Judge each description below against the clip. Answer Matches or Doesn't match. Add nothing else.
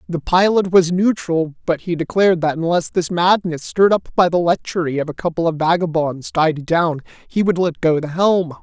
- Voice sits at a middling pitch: Matches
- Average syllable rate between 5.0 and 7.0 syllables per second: Matches